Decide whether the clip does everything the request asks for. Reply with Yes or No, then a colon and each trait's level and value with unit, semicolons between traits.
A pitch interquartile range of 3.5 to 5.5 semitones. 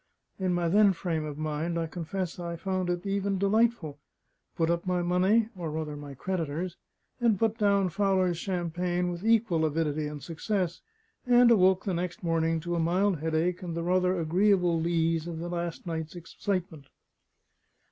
No: narrow, 2.6 semitones